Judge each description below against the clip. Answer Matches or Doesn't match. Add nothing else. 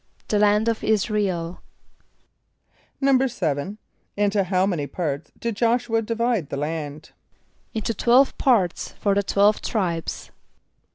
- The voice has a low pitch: Doesn't match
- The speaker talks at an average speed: Doesn't match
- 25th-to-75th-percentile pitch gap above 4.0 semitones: Matches